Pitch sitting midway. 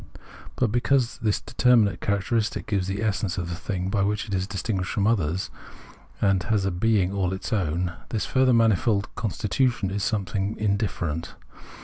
No: low, 100 Hz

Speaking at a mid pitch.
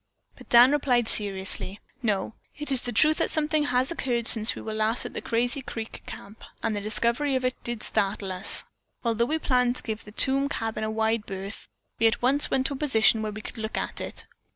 No: high, 230 Hz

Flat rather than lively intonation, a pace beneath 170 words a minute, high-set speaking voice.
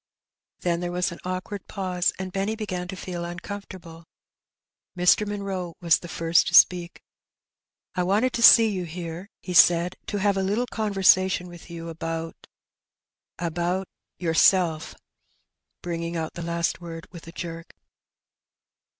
No: narrow, 2.2 semitones; average, 150 wpm; medium, 180 Hz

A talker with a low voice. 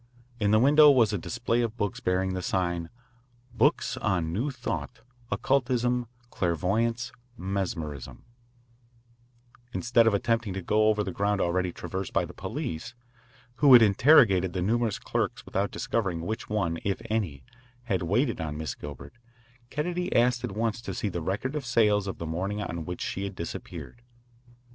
Yes: low, 105 Hz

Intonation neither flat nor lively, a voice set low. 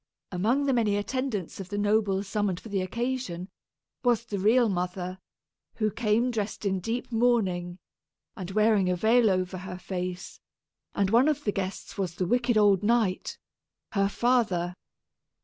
No: average, 4.0 semitones; high, 205 Hz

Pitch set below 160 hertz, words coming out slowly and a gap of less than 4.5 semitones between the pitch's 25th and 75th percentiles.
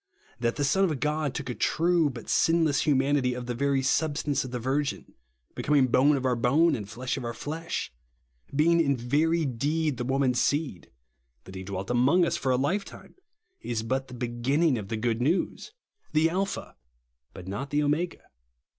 No: low, 135 Hz; average, 185 wpm; average, 4.0 semitones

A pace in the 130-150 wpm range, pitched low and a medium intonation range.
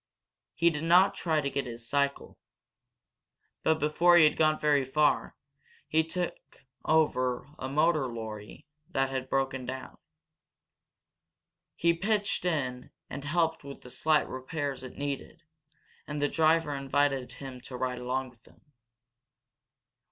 No: slow, 135 wpm; medium, 145 Hz; average, 3.4 semitones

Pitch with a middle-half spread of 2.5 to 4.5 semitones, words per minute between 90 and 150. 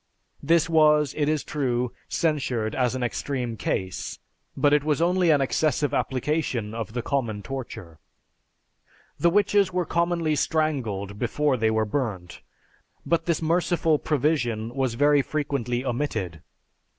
No: average, 5.0 semitones; slow, 135 wpm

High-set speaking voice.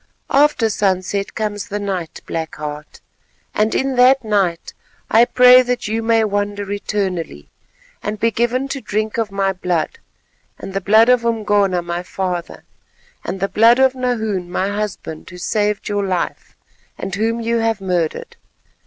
Yes: high, 205 Hz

